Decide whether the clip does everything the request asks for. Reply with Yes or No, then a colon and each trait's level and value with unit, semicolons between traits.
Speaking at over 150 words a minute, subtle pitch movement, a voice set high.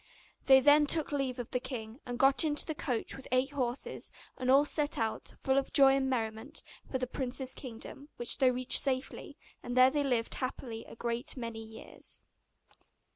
Yes: average, 185 wpm; narrow, 2.3 semitones; very high, 260 Hz